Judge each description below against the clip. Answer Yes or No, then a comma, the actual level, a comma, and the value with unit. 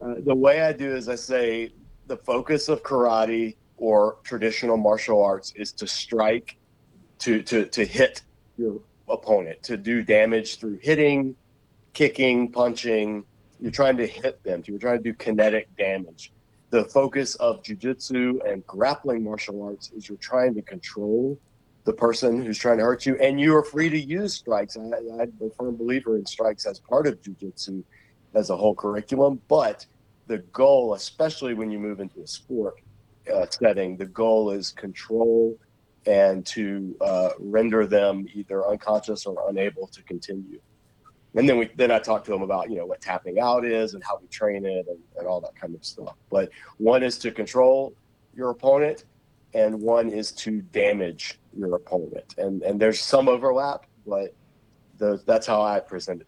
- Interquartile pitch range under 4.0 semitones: Yes, average, 3.5 semitones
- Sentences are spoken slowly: No, average, 175 wpm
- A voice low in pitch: Yes, low, 115 Hz